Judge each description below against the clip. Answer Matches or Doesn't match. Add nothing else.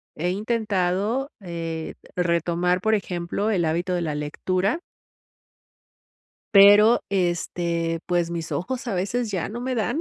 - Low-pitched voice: Doesn't match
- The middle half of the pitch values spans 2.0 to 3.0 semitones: Doesn't match